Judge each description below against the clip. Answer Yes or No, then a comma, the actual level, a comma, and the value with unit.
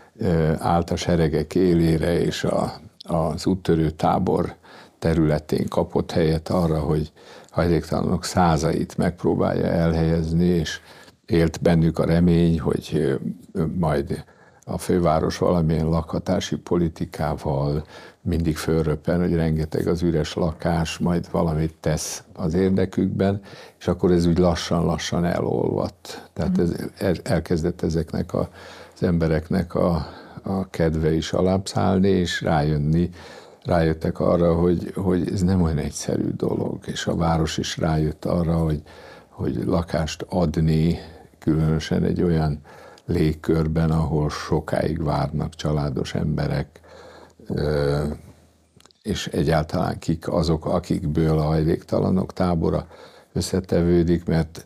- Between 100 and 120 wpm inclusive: Yes, average, 110 wpm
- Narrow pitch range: Yes, narrow, 1.8 semitones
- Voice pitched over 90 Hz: No, very low, 80 Hz